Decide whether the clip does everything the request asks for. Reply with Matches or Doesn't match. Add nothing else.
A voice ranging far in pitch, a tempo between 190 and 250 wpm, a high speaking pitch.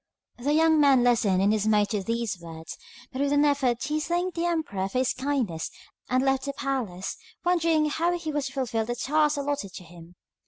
Matches